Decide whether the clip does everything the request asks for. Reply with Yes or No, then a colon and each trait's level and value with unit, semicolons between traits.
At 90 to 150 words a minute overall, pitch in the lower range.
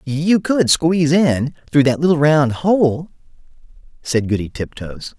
No: average, 140 wpm; medium, 145 Hz